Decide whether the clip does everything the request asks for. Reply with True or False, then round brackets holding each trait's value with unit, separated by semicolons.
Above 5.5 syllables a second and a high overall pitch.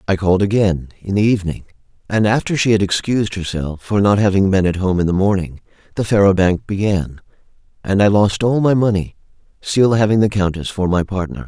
False (5.8 syllables/s; 100 Hz)